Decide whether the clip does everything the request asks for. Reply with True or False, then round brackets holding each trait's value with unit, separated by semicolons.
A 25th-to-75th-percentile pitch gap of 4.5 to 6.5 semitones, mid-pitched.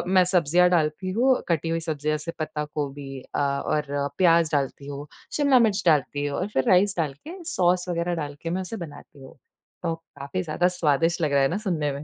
False (3.8 semitones; 165 Hz)